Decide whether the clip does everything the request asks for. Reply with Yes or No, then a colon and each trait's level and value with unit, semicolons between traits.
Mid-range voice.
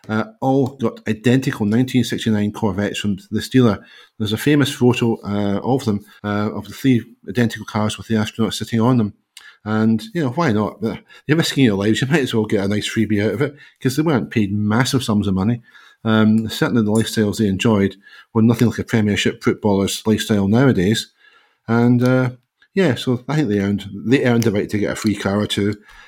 No: low, 110 Hz